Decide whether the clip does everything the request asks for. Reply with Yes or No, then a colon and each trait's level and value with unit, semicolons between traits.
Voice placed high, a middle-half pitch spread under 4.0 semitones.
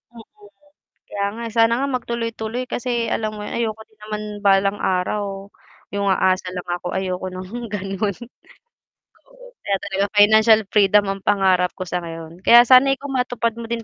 Yes: high, 210 Hz; average, 3.3 semitones